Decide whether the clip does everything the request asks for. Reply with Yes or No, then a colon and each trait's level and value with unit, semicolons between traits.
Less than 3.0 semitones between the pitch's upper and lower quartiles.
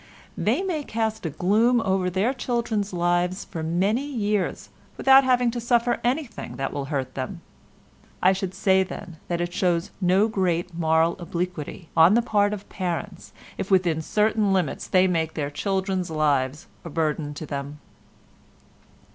No: average, 4.7 semitones